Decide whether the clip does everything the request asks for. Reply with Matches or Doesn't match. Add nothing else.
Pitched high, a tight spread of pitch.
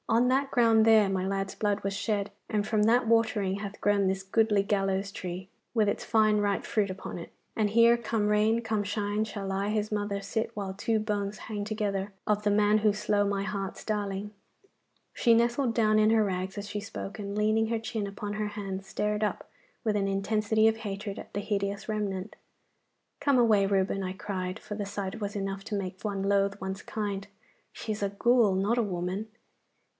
Matches